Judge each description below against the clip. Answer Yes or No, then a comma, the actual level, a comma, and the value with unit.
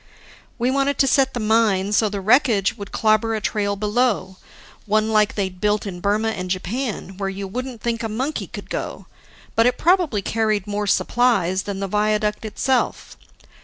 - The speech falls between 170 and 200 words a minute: Yes, average, 175 wpm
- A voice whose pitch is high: Yes, high, 215 Hz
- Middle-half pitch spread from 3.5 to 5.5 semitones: No, average, 2.9 semitones